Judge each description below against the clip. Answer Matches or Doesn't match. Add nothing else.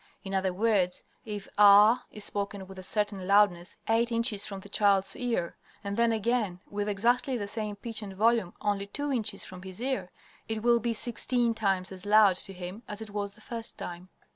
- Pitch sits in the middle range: Doesn't match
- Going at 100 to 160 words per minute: Doesn't match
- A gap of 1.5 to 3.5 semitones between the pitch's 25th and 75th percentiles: Matches